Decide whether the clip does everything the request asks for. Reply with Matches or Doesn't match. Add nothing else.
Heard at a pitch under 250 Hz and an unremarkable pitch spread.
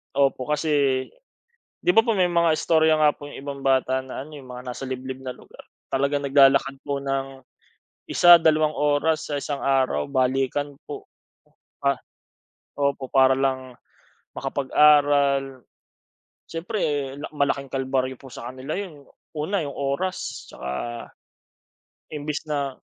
Doesn't match